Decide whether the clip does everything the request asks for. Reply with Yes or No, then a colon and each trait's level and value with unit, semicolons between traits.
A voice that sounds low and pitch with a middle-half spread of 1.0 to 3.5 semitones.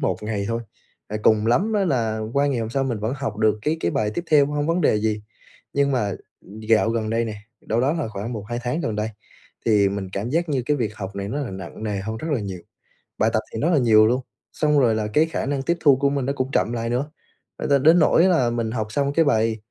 No: low, 120 Hz; average, 4.7 semitones